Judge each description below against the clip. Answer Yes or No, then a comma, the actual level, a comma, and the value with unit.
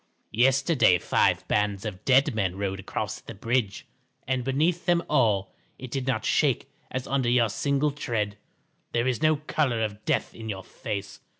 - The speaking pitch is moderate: No, low, 120 Hz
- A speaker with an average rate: Yes, average, 170 wpm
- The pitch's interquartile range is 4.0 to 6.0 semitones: Yes, average, 4.5 semitones